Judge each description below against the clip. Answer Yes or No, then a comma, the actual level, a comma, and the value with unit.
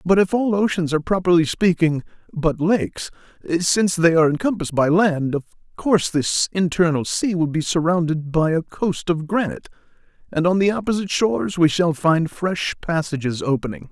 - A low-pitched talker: No, medium, 170 Hz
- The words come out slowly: No, average, 170 wpm